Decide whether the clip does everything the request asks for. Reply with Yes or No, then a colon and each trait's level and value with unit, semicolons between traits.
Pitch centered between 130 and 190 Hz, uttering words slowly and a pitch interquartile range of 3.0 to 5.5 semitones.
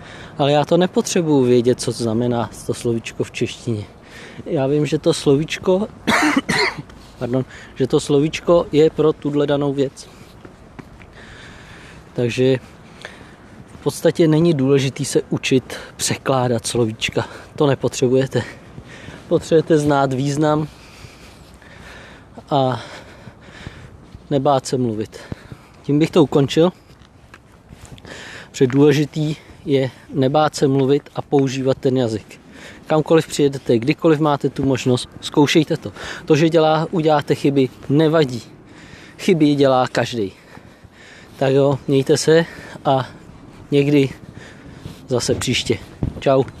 Yes: medium, 140 Hz; slow, 110 wpm; average, 3.5 semitones